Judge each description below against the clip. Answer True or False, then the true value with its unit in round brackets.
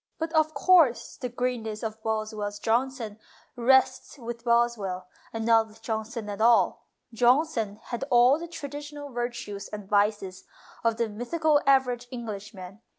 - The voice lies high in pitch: True (235 Hz)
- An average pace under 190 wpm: True (145 wpm)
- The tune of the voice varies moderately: True (3.4 semitones)